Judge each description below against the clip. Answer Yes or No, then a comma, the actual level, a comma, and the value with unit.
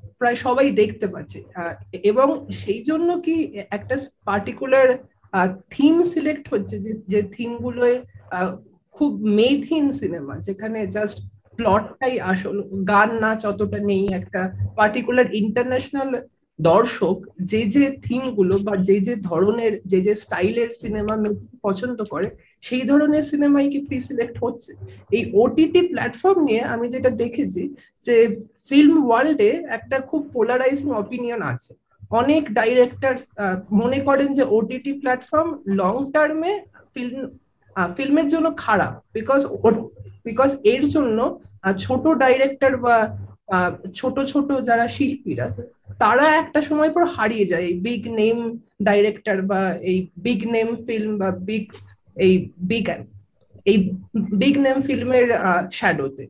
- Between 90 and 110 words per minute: No, fast, 120 wpm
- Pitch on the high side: Yes, high, 230 Hz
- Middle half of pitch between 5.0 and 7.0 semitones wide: Yes, average, 5.3 semitones